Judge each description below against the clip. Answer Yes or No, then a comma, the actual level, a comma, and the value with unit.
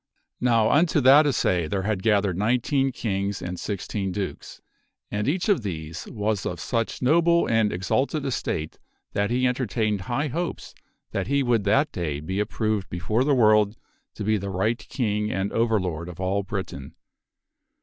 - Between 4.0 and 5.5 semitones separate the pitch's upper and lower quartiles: Yes, average, 4.6 semitones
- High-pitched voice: No, low, 105 Hz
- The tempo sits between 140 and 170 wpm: Yes, average, 165 wpm